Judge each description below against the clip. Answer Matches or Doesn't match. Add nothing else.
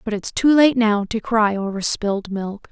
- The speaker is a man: Doesn't match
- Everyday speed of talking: Doesn't match